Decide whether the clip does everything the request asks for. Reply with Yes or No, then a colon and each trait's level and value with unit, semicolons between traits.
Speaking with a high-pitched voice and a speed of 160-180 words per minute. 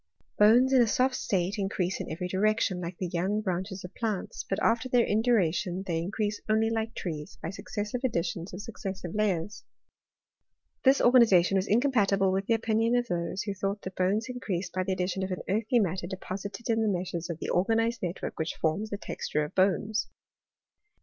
No: high, 195 Hz; average, 195 wpm